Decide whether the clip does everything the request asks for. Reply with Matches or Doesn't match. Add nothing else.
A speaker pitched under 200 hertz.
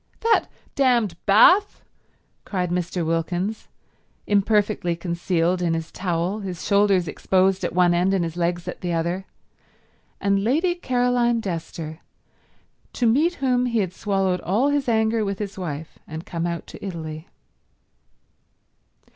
Matches